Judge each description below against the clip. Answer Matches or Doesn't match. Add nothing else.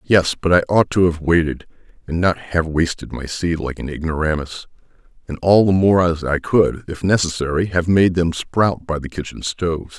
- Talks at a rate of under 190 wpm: Doesn't match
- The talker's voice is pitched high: Doesn't match